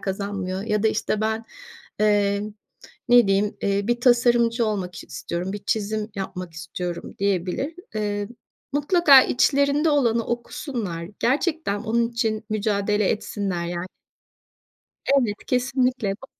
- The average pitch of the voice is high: Yes, high, 215 Hz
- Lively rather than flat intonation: No, average, 3.4 semitones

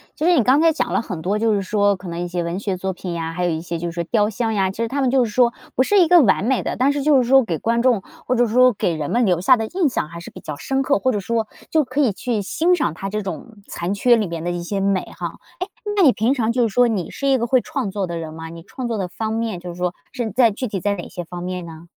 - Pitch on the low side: No, high, 210 Hz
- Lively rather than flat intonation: Yes, wide, 6.1 semitones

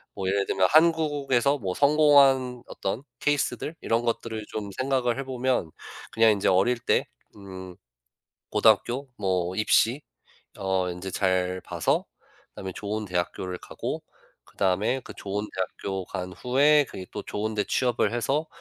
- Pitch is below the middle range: Yes, low, 110 Hz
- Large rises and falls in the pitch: Yes, wide, 5.8 semitones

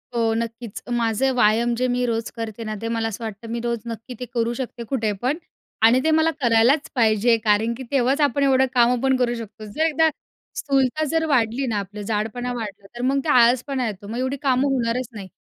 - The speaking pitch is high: Yes, high, 235 Hz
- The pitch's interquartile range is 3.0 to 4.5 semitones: No, narrow, 2.6 semitones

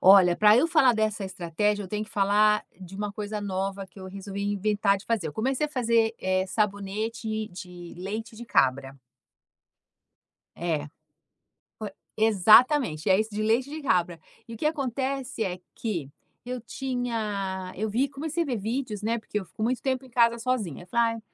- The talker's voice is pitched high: Yes, high, 215 Hz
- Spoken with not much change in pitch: No, average, 3.6 semitones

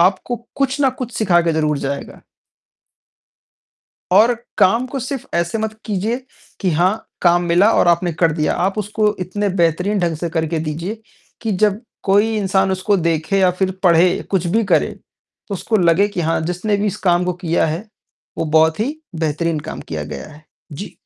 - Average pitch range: Yes, average, 3.9 semitones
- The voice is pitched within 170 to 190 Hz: Yes, medium, 185 Hz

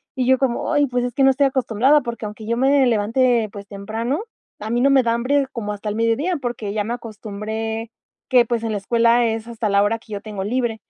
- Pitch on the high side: Yes, high, 230 Hz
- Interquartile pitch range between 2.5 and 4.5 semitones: Yes, average, 2.8 semitones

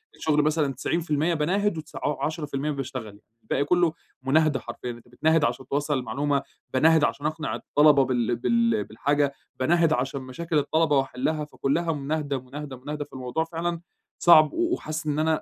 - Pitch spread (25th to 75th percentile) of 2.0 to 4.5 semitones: Yes, average, 2.9 semitones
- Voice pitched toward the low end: No, medium, 150 Hz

